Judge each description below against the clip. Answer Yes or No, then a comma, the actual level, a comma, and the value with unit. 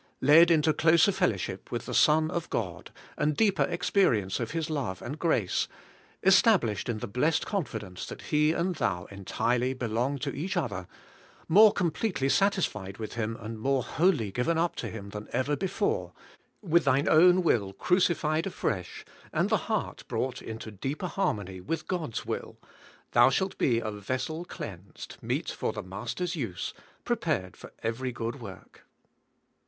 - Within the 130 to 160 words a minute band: No, average, 170 wpm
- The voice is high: No, low, 135 Hz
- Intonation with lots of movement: Yes, wide, 7.7 semitones